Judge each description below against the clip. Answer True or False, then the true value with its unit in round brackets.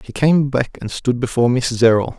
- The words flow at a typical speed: False (220 wpm)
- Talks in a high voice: False (125 Hz)